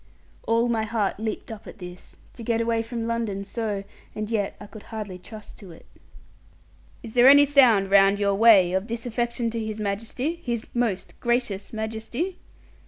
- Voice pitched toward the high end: Yes, high, 225 Hz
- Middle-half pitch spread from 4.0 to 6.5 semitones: No, narrow, 2.5 semitones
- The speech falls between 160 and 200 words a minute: Yes, average, 170 wpm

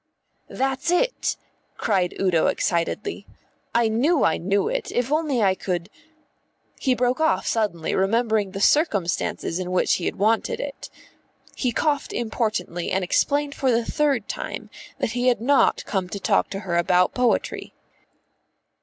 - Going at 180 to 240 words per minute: No, average, 155 wpm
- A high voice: Yes, high, 225 Hz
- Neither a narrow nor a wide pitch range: No, wide, 6.1 semitones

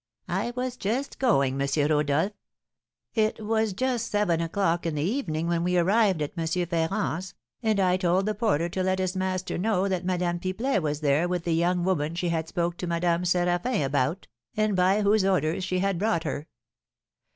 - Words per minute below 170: No, average, 185 wpm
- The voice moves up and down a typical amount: Yes, average, 3.1 semitones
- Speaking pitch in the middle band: Yes, medium, 180 Hz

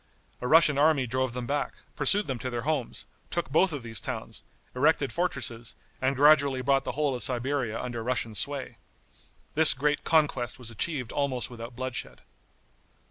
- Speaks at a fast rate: No, average, 165 wpm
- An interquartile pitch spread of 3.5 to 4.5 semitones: No, average, 3.1 semitones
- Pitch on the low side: Yes, low, 130 Hz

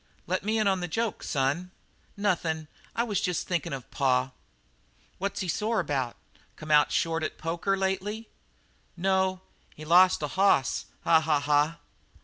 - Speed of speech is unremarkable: Yes, average, 155 wpm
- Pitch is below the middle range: No, medium, 175 Hz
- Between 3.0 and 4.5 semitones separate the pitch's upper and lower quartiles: Yes, average, 4.2 semitones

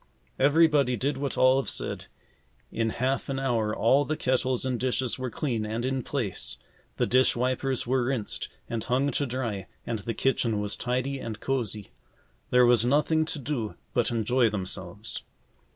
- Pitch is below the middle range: Yes, low, 125 Hz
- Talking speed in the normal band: Yes, average, 165 wpm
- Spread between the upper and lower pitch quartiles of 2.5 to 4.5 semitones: Yes, average, 2.8 semitones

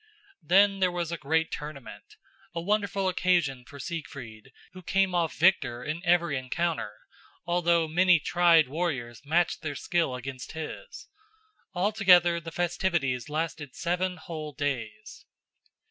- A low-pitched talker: No, medium, 165 Hz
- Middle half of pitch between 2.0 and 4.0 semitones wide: Yes, average, 3.7 semitones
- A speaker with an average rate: No, slow, 130 wpm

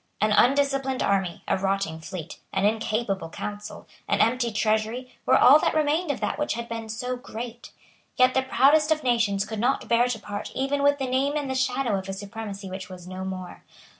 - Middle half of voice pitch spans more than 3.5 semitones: Yes, average, 4.8 semitones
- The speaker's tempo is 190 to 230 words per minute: Yes, average, 200 wpm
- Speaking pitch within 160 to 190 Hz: No, high, 230 Hz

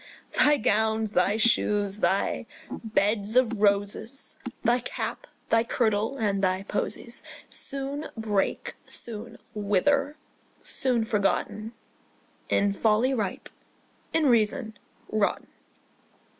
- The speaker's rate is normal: No, slow, 100 wpm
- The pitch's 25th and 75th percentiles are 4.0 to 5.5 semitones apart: No, average, 2.9 semitones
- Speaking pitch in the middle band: No, high, 220 Hz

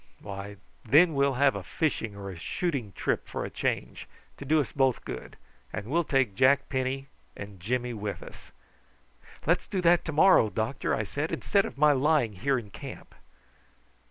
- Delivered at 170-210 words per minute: Yes, average, 180 wpm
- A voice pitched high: No, low, 135 Hz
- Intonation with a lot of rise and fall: Yes, wide, 5.8 semitones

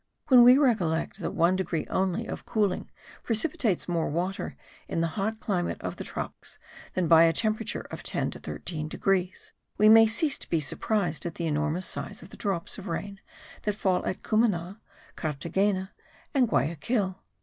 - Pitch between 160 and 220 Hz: Yes, high, 190 Hz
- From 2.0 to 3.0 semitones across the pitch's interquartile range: No, average, 4.3 semitones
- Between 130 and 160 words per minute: No, average, 170 wpm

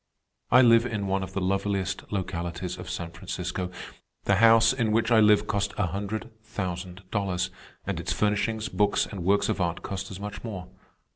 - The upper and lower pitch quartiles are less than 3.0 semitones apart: Yes, narrow, 2.6 semitones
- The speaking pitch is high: No, low, 100 Hz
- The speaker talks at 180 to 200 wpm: Yes, average, 185 wpm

